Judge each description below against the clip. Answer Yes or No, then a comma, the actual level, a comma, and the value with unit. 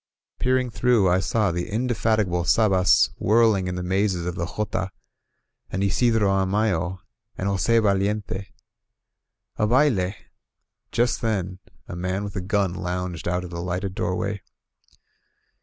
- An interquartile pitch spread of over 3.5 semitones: No, average, 2.9 semitones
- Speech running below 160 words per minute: Yes, average, 140 wpm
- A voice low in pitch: Yes, very low, 95 Hz